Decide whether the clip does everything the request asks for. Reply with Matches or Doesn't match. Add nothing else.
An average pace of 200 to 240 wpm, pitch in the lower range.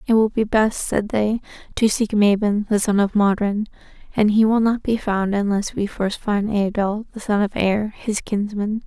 Doesn't match